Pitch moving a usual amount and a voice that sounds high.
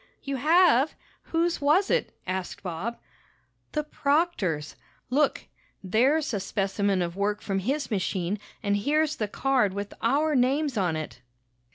No: wide, 7.4 semitones; high, 235 Hz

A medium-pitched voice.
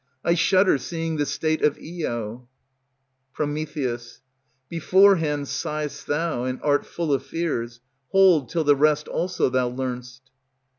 Yes: medium, 150 Hz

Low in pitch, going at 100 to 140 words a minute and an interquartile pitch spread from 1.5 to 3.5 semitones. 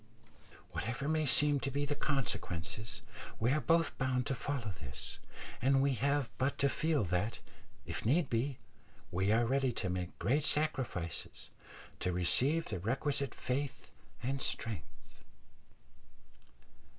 No: low, 130 Hz; slow, 135 wpm; average, 4.4 semitones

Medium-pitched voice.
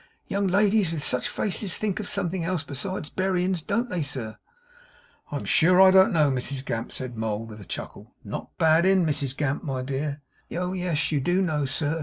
Yes: medium, 165 Hz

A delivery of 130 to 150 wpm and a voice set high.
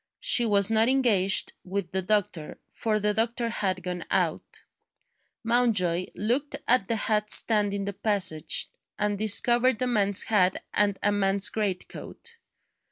Yes: average, 145 wpm; high, 210 Hz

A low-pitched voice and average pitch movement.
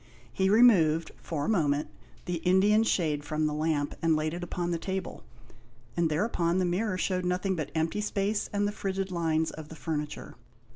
No: medium, 175 Hz; average, 3.5 semitones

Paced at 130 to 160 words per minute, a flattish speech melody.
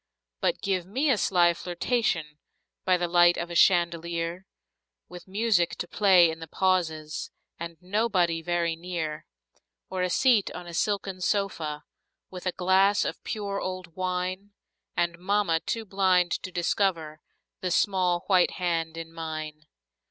Yes: average, 145 wpm; narrow, 2.3 semitones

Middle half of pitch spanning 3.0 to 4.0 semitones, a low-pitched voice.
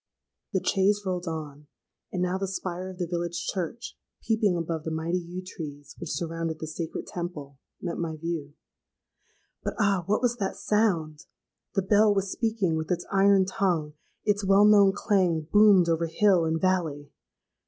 No: average, 3.4 semitones; medium, 180 Hz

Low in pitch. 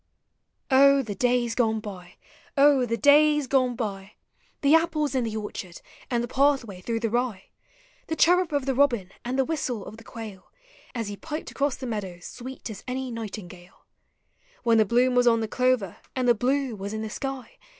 No: high, 245 Hz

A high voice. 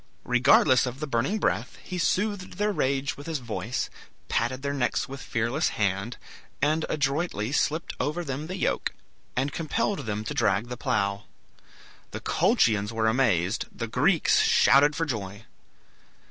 No: low, 135 Hz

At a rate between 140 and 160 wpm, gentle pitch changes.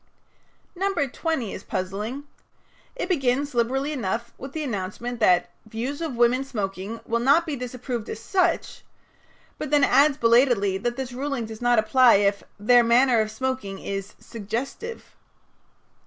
No: average, 145 wpm; average, 4.0 semitones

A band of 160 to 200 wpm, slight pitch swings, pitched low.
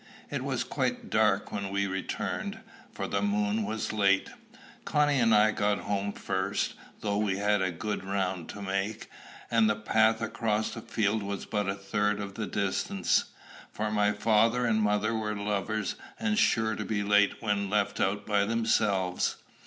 Yes: average, 170 wpm; narrow, 1.5 semitones; low, 105 Hz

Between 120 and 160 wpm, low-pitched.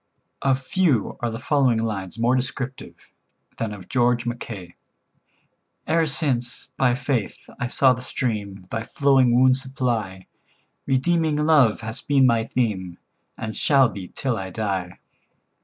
Yes: average, 140 wpm; low, 120 Hz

